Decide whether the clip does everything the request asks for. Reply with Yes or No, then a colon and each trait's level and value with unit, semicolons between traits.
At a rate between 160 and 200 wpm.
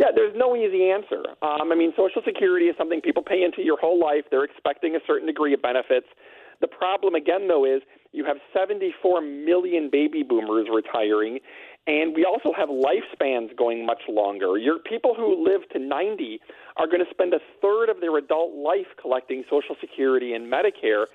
Yes: average, 185 wpm